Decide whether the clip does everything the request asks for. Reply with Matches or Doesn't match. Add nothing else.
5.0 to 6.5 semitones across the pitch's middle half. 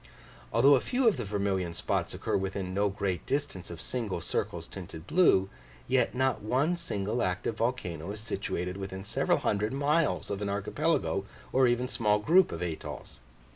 Matches